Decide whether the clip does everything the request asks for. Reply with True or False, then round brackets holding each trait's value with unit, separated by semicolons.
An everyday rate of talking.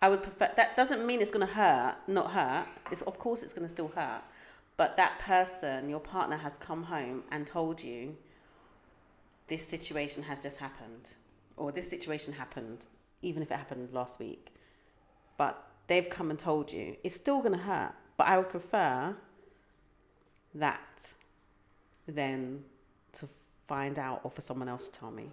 True (165 wpm)